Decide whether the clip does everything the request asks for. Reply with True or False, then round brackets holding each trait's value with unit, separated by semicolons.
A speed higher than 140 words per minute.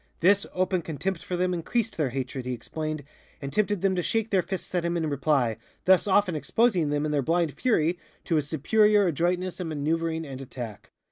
True (200 wpm)